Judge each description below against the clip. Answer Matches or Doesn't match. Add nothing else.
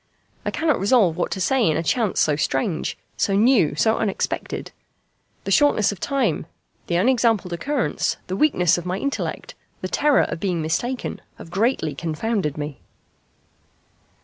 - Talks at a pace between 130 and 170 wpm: Matches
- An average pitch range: Doesn't match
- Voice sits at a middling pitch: Doesn't match